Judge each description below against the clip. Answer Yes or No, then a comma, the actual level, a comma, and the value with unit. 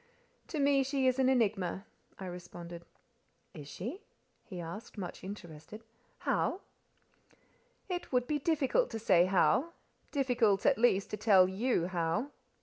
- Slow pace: Yes, slow, 130 wpm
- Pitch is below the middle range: No, high, 210 Hz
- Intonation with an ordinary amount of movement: No, wide, 6.7 semitones